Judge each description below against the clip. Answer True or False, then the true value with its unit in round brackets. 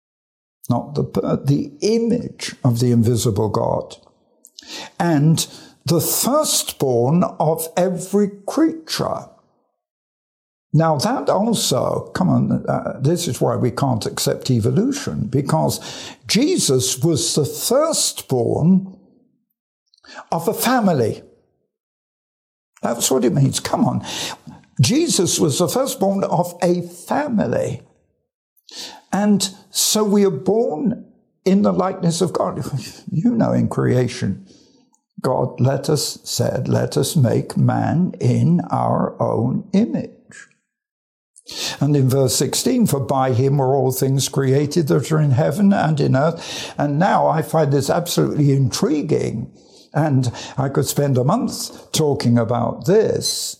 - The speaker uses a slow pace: True (120 wpm)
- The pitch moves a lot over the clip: True (6.8 semitones)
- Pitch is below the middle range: False (160 Hz)